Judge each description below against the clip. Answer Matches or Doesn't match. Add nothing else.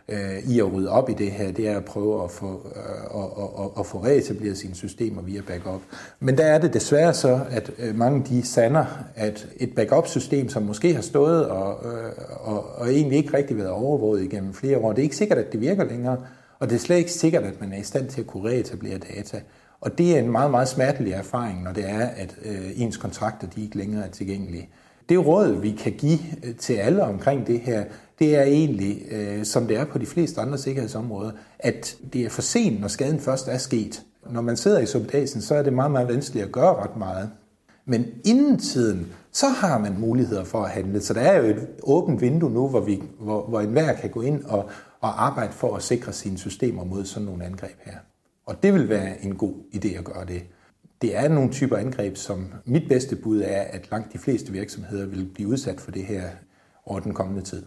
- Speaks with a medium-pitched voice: Doesn't match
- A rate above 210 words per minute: Matches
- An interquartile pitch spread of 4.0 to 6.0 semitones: Matches